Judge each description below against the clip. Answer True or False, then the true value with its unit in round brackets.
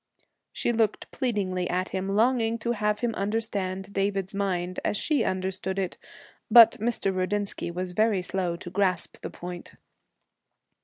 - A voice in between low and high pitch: False (195 Hz)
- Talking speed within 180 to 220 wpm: False (145 wpm)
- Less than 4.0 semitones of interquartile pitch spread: True (2.9 semitones)